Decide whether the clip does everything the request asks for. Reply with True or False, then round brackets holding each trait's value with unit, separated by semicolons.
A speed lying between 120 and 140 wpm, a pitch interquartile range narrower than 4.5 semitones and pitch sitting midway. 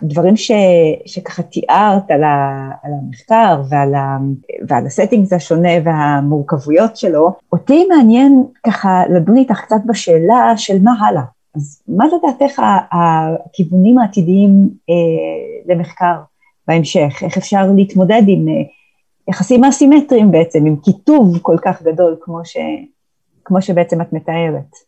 False (125 wpm; 5.1 semitones; 180 Hz)